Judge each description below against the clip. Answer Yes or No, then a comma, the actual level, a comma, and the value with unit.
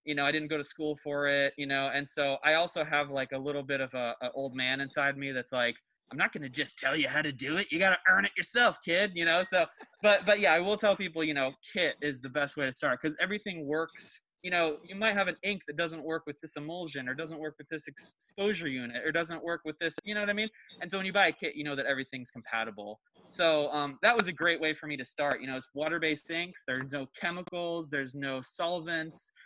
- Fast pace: Yes, fast, 270 wpm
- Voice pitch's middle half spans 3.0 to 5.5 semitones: Yes, average, 3.6 semitones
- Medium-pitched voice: Yes, medium, 155 Hz